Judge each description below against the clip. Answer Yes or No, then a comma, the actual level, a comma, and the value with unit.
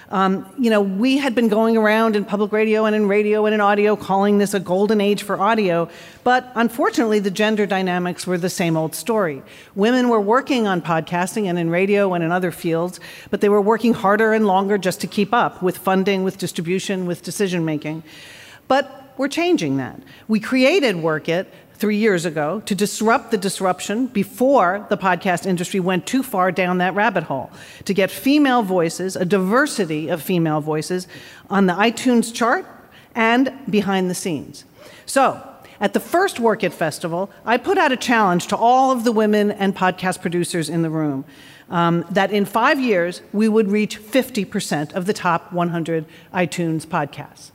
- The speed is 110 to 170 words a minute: No, average, 180 wpm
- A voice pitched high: Yes, high, 200 Hz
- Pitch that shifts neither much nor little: Yes, average, 3.6 semitones